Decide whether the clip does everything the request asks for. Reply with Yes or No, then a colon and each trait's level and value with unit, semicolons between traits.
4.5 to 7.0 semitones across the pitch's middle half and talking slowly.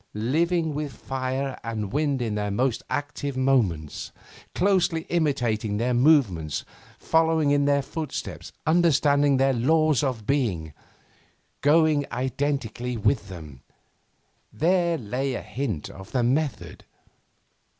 Yes: average, 5.0 semitones; slow, 115 wpm